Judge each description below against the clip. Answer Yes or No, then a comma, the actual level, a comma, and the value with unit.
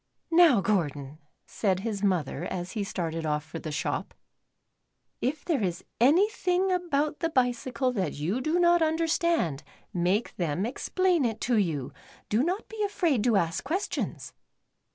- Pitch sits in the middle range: No, high, 235 Hz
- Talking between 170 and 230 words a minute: No, average, 155 wpm